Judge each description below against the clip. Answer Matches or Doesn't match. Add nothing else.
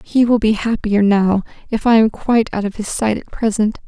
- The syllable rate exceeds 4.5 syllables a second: Matches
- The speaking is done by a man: Doesn't match